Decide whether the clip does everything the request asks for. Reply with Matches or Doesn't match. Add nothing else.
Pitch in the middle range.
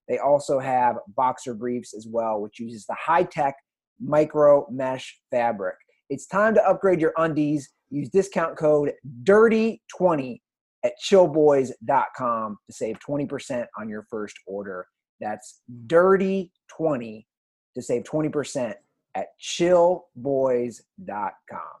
Matches